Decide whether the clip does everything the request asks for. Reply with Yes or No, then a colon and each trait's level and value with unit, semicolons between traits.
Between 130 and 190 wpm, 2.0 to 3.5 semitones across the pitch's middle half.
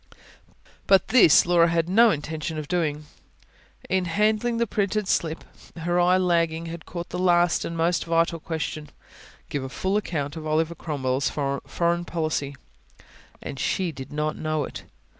Yes: average, 155 wpm; narrow, 2.5 semitones